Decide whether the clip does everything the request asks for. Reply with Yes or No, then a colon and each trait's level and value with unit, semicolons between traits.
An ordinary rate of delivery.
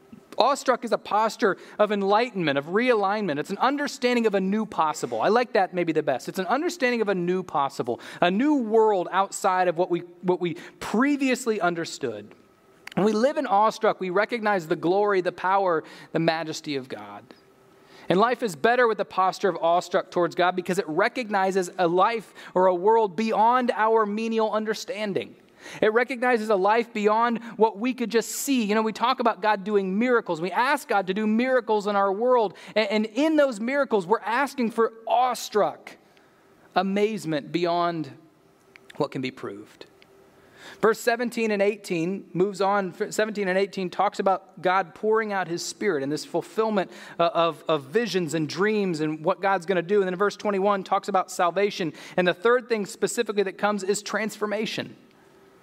No: fast, 180 wpm